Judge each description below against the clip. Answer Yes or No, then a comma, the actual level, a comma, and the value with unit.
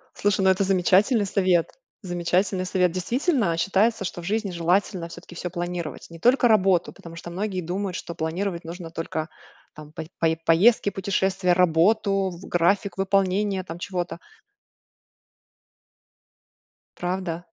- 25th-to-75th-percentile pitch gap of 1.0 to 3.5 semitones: Yes, narrow, 2.4 semitones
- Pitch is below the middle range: No, medium, 185 Hz